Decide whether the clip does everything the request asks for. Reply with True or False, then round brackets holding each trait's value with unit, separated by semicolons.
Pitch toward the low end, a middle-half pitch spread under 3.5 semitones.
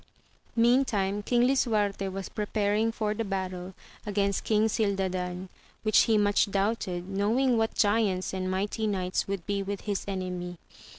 False (200 Hz; 2.4 semitones)